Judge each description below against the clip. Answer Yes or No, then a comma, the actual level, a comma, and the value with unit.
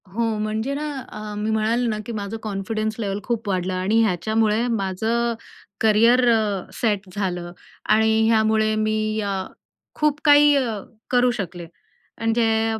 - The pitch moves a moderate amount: No, narrow, 1.8 semitones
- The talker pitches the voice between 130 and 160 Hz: No, high, 220 Hz